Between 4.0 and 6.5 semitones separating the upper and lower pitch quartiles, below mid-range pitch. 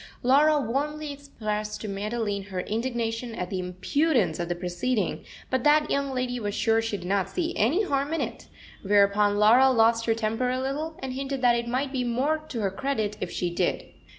No: average, 4.8 semitones; high, 235 Hz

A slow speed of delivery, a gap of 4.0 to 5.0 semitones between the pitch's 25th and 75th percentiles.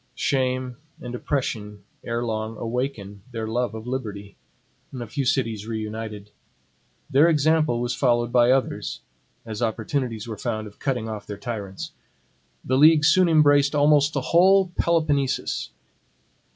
Yes: slow, 130 wpm; average, 4.4 semitones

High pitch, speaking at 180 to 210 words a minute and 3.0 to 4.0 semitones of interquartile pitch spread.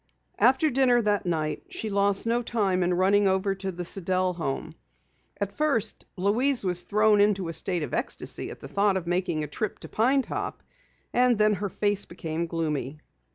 Yes: high, 195 Hz; average, 185 wpm; average, 3.5 semitones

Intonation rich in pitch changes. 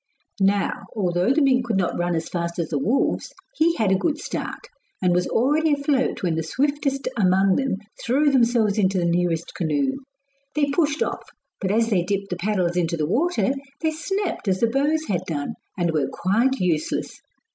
Yes: wide, 7.7 semitones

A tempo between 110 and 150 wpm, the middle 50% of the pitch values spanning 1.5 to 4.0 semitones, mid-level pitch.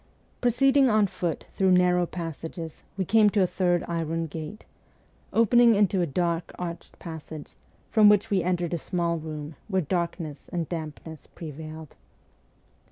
Yes: average, 145 wpm; average, 3.3 semitones; medium, 175 Hz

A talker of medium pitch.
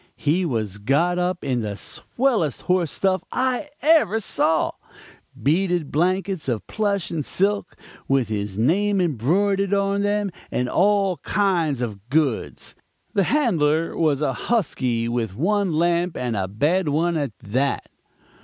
Yes: medium, 170 Hz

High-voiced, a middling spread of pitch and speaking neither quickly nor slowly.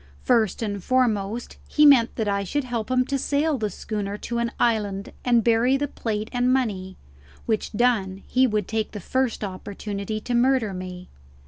Yes: high, 225 Hz; average, 3.7 semitones; average, 180 wpm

